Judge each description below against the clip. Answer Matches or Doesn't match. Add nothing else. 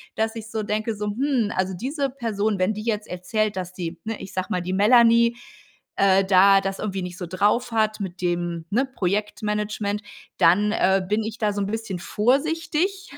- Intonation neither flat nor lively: Matches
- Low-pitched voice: Doesn't match